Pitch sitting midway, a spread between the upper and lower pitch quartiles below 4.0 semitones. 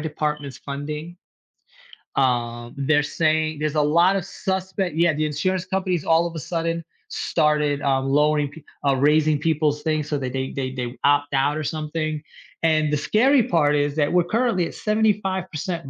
Yes: medium, 155 Hz; average, 2.9 semitones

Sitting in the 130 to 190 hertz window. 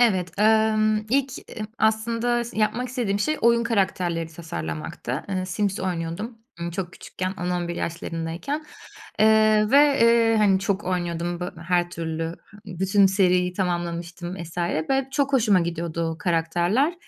Yes: medium, 185 Hz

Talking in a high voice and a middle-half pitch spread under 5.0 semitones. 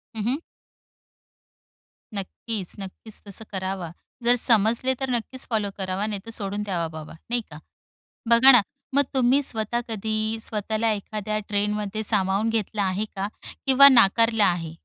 Yes: high, 215 Hz; average, 2.8 semitones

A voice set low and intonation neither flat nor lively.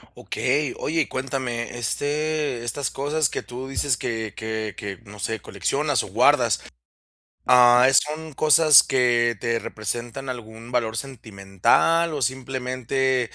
Yes: low, 125 Hz; average, 3.1 semitones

